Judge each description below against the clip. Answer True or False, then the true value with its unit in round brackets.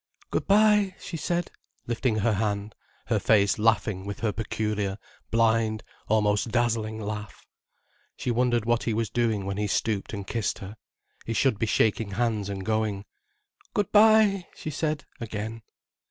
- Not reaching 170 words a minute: True (155 wpm)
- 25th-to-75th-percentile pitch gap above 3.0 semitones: False (2.5 semitones)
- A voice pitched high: False (110 Hz)